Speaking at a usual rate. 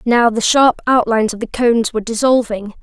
Yes: average, 190 wpm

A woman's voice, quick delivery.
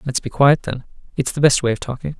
Yes: female; fast, 275 wpm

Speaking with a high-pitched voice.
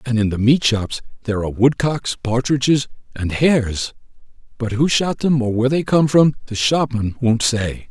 No: low, 125 Hz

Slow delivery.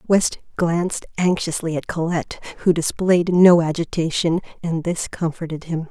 Yes: slow, 130 wpm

